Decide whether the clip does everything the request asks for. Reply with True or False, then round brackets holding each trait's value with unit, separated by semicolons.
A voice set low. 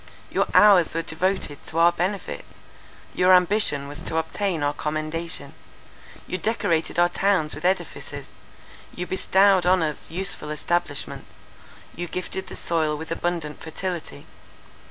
False (175 Hz)